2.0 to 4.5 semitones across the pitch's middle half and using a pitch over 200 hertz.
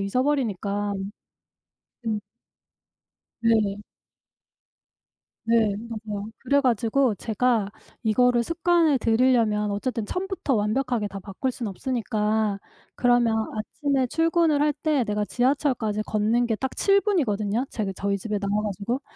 Yes: average, 4.0 semitones; high, 230 Hz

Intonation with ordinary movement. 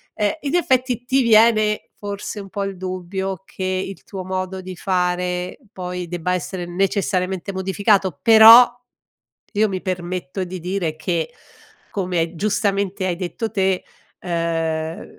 No: narrow, 2.2 semitones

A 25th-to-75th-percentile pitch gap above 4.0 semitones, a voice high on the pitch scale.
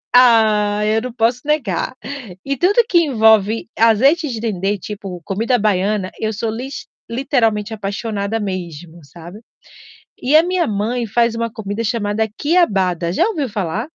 No: average, 3.6 semitones; high, 220 Hz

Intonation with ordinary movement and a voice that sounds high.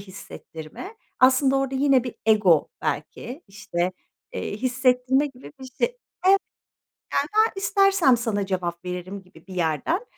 No: wide, 6.5 semitones; very high, 250 Hz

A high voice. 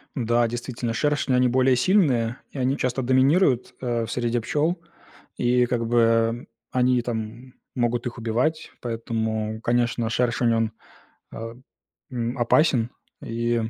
No: low, 120 Hz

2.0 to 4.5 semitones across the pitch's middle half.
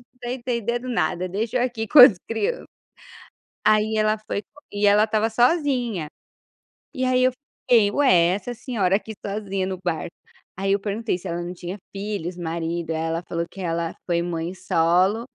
No: average, 5.0 semitones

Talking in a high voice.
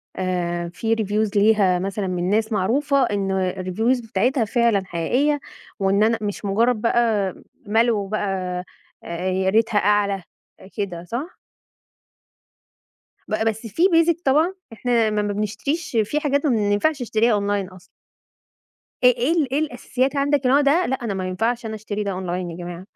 Yes: high, 215 Hz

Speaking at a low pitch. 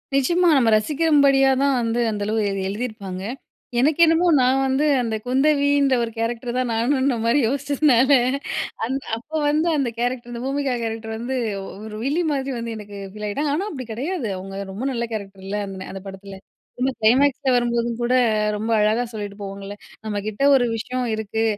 No: high, 240 Hz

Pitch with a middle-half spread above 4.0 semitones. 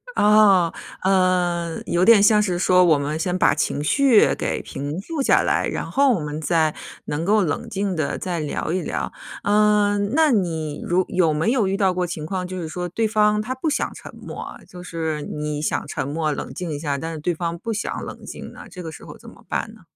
Yes: average, 4.6 semitones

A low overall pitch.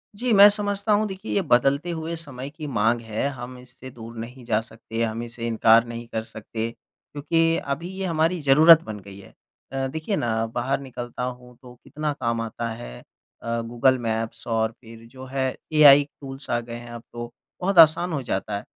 Yes: low, 125 Hz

